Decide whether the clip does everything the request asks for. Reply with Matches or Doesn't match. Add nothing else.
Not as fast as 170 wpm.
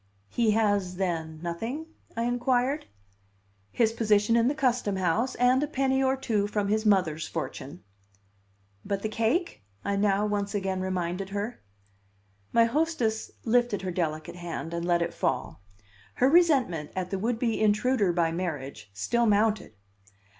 Matches